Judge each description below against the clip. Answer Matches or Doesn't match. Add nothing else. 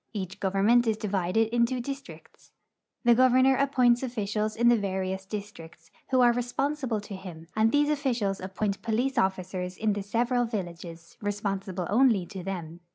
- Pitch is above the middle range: Matches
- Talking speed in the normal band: Matches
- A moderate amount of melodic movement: Matches